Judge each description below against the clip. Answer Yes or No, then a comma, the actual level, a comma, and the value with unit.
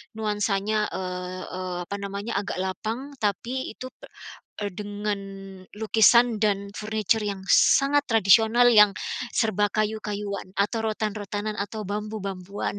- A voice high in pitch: Yes, high, 210 Hz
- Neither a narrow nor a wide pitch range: No, narrow, 1.7 semitones